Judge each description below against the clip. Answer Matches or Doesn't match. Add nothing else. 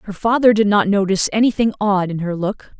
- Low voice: Doesn't match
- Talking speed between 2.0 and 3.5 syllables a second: Doesn't match